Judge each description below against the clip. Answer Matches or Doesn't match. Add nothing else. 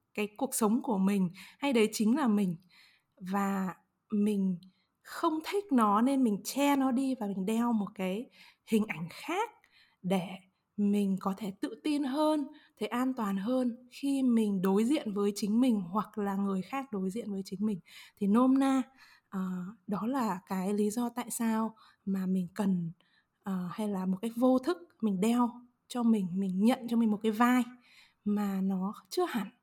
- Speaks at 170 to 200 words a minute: Matches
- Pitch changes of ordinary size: Matches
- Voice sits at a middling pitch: Doesn't match